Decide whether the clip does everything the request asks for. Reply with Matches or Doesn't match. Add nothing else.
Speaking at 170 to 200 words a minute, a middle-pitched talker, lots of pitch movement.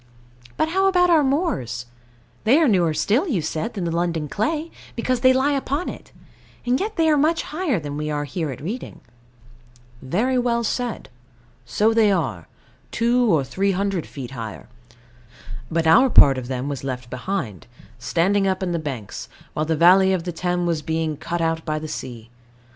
Matches